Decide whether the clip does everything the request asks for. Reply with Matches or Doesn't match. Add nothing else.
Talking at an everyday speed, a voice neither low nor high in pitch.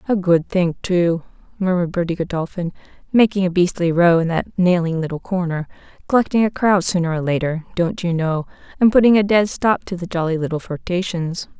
Matches